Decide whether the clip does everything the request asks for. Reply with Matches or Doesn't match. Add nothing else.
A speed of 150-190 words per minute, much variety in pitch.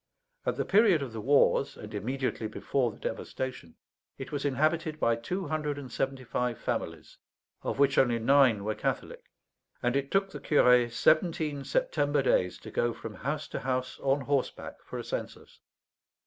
Doesn't match